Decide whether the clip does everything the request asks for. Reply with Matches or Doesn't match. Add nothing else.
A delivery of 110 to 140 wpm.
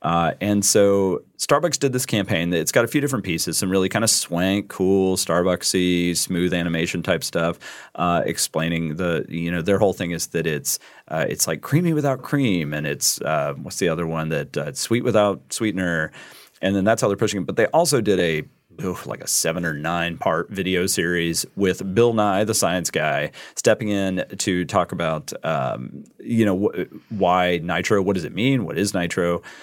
Doesn't match